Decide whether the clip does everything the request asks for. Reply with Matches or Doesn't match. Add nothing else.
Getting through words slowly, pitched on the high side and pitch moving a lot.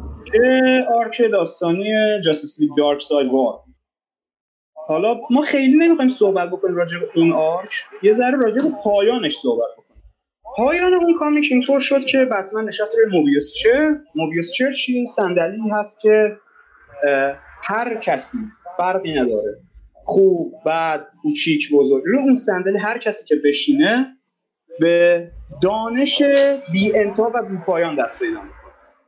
Doesn't match